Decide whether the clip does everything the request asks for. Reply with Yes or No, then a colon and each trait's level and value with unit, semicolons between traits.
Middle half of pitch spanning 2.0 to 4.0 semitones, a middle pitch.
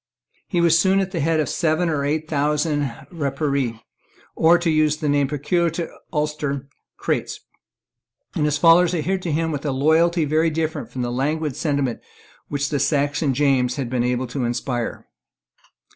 Yes: average, 2.8 semitones; medium, 150 Hz